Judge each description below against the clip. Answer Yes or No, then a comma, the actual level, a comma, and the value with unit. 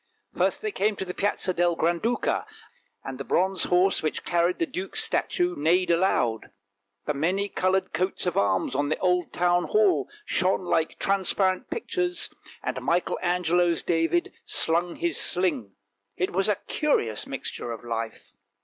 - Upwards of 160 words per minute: No, average, 155 wpm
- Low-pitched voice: No, medium, 180 Hz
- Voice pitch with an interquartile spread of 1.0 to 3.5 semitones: Yes, average, 2.7 semitones